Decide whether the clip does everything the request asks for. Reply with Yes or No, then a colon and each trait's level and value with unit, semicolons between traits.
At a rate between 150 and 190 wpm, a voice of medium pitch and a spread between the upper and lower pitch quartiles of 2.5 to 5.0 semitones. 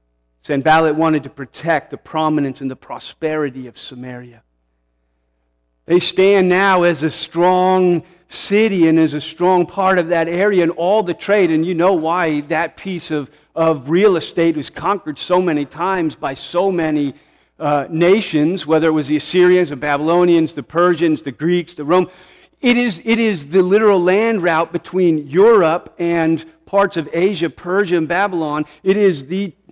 Yes: average, 170 wpm; medium, 165 Hz; average, 3.5 semitones